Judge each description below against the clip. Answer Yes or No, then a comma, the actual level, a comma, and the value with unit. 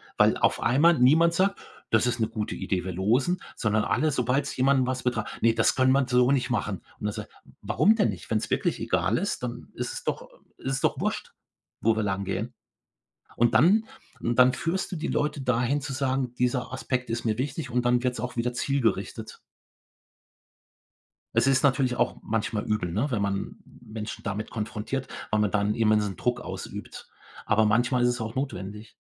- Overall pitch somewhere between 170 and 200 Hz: No, low, 125 Hz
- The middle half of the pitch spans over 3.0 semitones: Yes, average, 3.7 semitones